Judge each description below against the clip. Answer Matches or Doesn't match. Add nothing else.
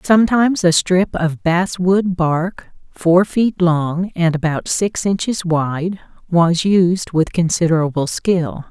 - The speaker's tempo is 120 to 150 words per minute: Matches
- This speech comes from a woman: Matches